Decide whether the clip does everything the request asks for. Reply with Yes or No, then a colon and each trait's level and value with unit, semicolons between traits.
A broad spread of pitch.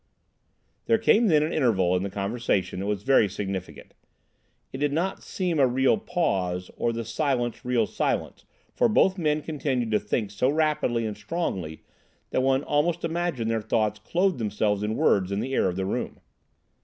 Yes: wide, 7.0 semitones